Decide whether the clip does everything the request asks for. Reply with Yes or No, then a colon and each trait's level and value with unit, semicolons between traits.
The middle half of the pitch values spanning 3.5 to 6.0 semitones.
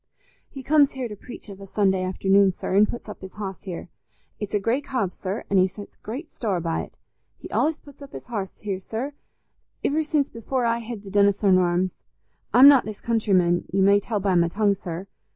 Yes: average, 4.0 semitones